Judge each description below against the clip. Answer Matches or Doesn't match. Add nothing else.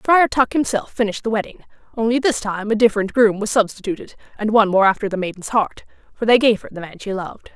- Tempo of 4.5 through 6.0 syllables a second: Doesn't match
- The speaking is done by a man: Doesn't match